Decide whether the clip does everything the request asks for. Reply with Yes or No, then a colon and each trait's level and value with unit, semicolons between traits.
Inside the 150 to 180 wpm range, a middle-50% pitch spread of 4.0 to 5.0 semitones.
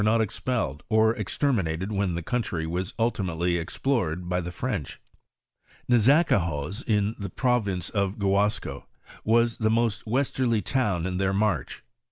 No: average, 140 wpm; average, 4.7 semitones